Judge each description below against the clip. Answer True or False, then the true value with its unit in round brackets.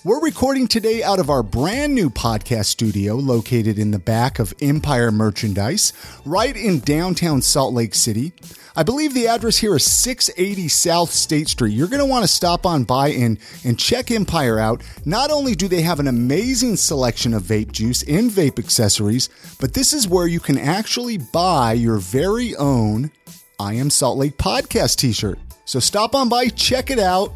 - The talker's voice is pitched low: False (145 Hz)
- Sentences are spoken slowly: False (185 wpm)